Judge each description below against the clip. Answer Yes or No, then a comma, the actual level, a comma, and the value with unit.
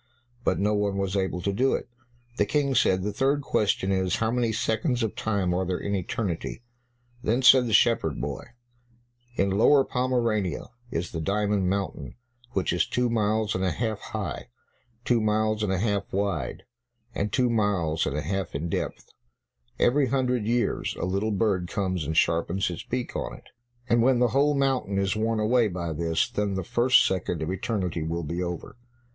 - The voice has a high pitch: No, low, 105 Hz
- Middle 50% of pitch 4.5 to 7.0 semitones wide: No, average, 4.1 semitones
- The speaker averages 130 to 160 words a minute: No, average, 185 wpm